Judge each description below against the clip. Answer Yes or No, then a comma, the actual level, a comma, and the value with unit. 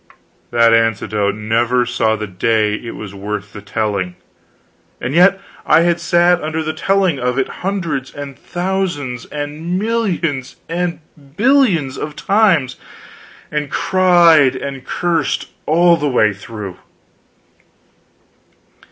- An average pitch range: No, wide, 7.3 semitones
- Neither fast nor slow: No, slow, 125 wpm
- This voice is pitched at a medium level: Yes, medium, 145 Hz